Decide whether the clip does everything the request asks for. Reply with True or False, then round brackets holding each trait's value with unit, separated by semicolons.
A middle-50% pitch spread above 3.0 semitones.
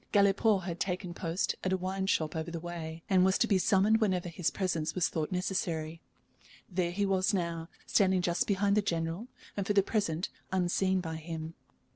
False (2.7 semitones)